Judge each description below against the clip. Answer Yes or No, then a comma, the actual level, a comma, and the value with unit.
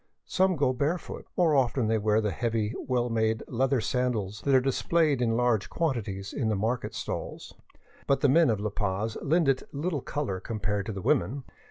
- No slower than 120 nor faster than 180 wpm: No, average, 190 wpm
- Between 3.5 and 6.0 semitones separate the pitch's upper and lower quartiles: Yes, average, 4.4 semitones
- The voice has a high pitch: No, low, 120 Hz